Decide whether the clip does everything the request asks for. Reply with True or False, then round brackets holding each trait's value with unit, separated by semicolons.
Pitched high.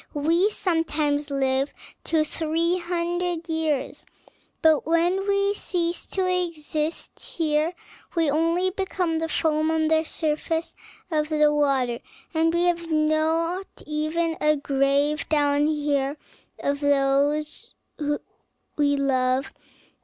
True (315 Hz)